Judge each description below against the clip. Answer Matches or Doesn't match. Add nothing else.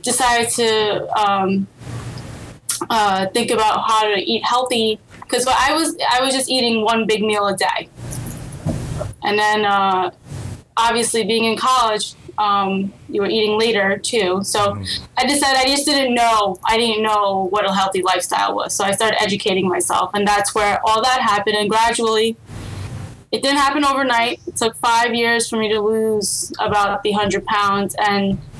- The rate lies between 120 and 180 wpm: Matches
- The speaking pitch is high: Matches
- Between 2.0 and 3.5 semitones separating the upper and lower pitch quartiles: Matches